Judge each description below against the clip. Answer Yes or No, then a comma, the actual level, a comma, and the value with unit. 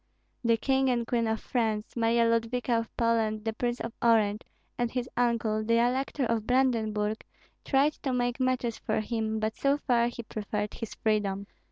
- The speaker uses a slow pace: No, average, 175 wpm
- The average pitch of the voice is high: Yes, high, 230 Hz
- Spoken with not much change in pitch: Yes, narrow, 2.0 semitones